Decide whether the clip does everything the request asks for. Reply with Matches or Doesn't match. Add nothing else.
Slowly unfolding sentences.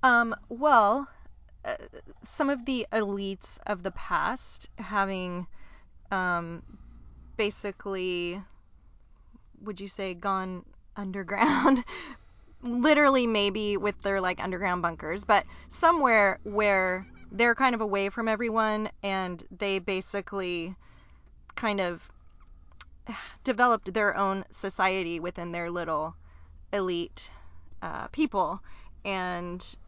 Matches